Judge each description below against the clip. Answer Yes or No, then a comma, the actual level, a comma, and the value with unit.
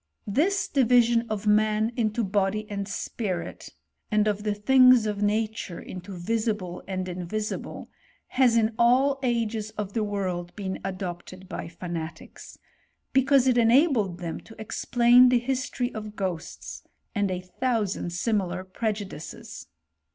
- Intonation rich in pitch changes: No, average, 3.9 semitones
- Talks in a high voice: Yes, high, 215 Hz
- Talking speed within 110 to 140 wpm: Yes, slow, 135 wpm